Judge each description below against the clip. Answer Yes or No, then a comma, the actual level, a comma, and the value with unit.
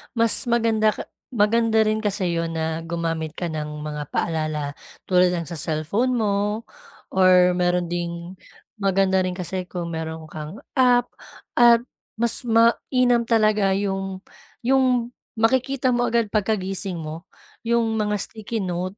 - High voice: Yes, high, 195 Hz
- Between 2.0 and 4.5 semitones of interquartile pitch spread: No, average, 5.1 semitones